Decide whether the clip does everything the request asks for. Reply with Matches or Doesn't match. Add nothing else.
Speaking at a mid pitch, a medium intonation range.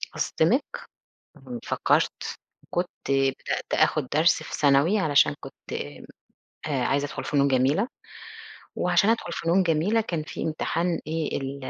Matches